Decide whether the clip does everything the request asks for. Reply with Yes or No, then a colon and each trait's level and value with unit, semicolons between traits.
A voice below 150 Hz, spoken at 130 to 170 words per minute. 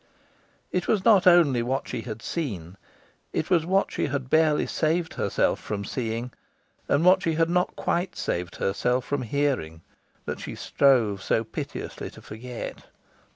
Yes: low, 135 Hz; average, 155 wpm